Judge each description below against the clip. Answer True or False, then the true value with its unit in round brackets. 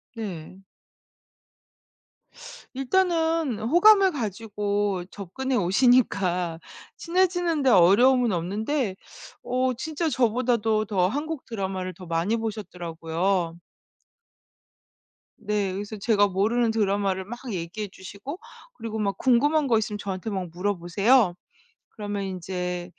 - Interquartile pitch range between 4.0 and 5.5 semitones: True (5.1 semitones)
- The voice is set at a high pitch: True (210 Hz)